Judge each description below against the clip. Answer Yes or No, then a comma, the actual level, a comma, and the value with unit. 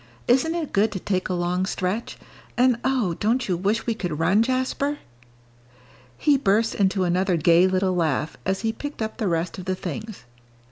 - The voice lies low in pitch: No, high, 195 Hz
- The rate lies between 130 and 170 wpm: No, average, 185 wpm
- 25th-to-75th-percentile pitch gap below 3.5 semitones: No, average, 4.4 semitones